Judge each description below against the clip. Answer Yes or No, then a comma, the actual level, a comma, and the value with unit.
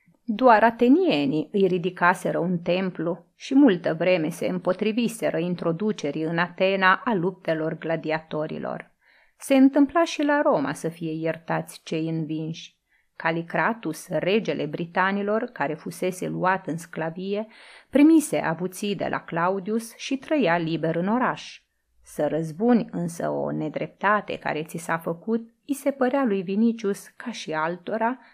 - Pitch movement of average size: No, wide, 5.9 semitones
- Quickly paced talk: No, average, 130 wpm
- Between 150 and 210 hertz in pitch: Yes, medium, 185 Hz